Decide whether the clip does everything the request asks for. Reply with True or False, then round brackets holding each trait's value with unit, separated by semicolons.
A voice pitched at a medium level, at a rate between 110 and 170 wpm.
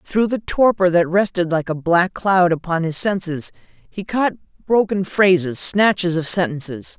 True (180 Hz; 165 wpm)